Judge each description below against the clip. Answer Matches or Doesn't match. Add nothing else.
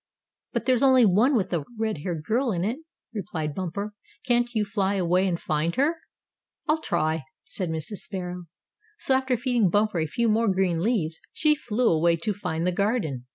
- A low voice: Doesn't match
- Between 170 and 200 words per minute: Matches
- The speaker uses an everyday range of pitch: Doesn't match